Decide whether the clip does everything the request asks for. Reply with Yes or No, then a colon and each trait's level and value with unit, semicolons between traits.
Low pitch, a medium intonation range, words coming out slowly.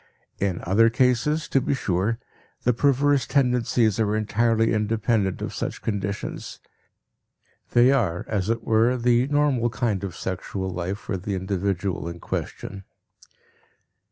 Yes: low, 110 Hz; average, 4.1 semitones; slow, 130 wpm